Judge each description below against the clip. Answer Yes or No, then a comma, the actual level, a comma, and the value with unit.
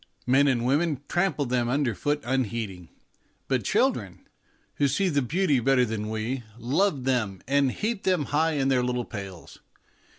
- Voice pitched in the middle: No, low, 130 Hz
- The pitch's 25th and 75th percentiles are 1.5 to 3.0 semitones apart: No, average, 3.6 semitones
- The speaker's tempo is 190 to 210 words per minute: No, average, 160 wpm